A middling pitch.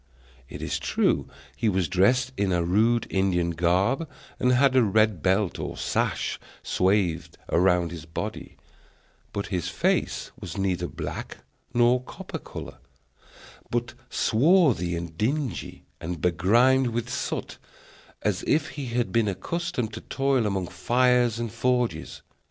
No: low, 110 Hz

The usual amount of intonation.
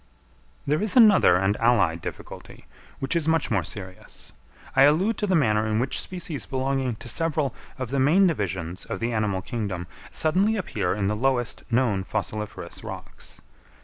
No: wide, 7.3 semitones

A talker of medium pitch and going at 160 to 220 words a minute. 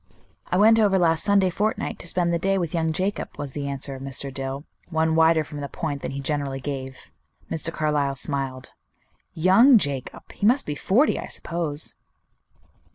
Yes: medium, 160 Hz; average, 180 wpm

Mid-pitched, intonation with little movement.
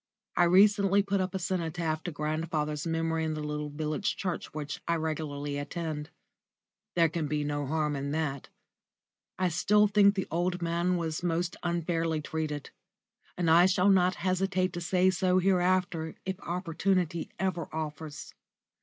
No: medium, 170 Hz; average, 3.0 semitones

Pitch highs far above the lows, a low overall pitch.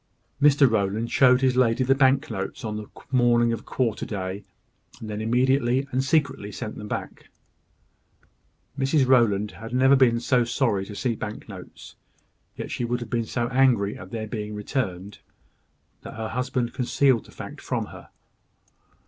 No: average, 3.5 semitones; low, 120 Hz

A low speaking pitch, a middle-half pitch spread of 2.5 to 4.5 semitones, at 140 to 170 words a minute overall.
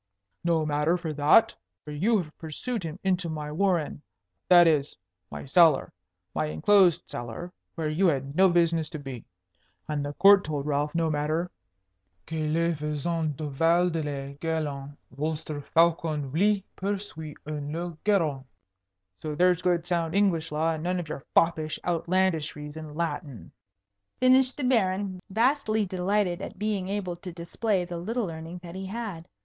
No: medium, 165 Hz; average, 3.6 semitones; average, 160 wpm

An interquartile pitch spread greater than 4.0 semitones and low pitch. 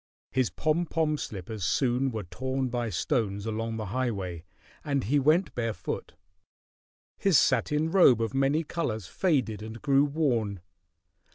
Yes: average, 5.1 semitones; low, 125 Hz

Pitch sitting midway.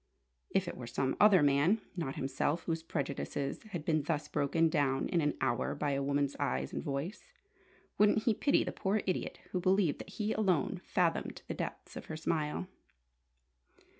Yes: medium, 155 Hz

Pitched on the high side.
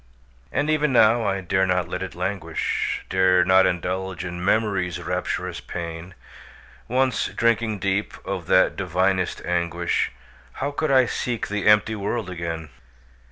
No: very low, 95 Hz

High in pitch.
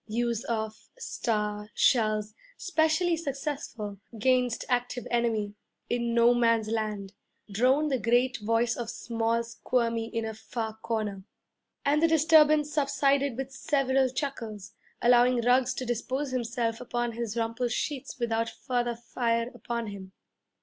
Yes: high, 235 Hz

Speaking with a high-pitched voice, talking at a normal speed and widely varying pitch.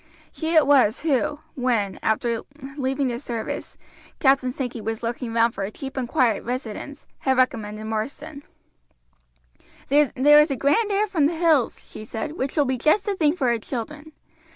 No: very high, 265 Hz; average, 175 wpm; average, 4.3 semitones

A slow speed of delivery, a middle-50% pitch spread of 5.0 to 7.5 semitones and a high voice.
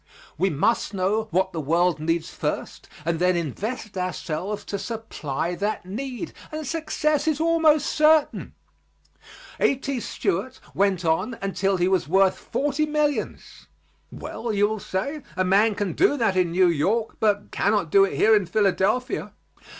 No: average, 150 wpm; wide, 5.6 semitones; high, 200 Hz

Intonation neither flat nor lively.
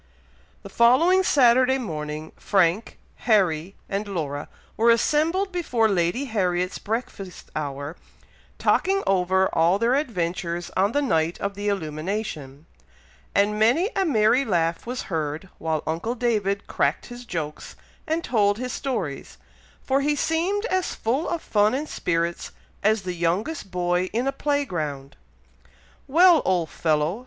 No: wide, 7.3 semitones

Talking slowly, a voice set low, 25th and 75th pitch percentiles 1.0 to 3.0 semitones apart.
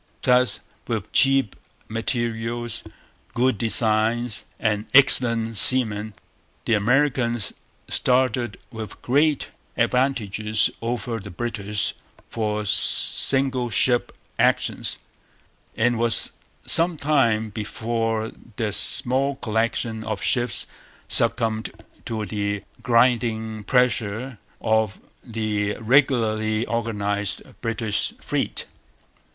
Yes: slow, 90 wpm; low, 115 Hz; narrow, 2.4 semitones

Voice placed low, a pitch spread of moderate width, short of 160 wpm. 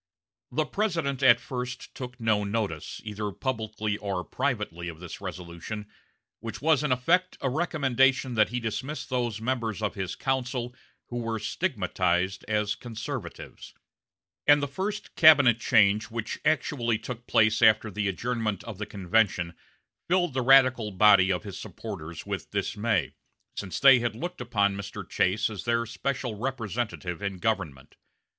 Yes: low, 115 Hz; average, 4.2 semitones; average, 150 wpm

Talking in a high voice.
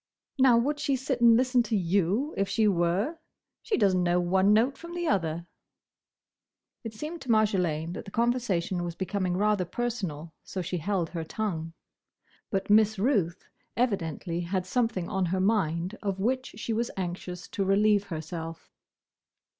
Yes: high, 195 Hz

